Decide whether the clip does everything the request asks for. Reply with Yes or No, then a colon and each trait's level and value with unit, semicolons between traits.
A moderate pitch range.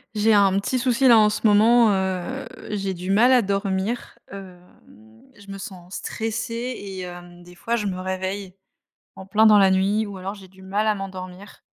No: narrow, 2.3 semitones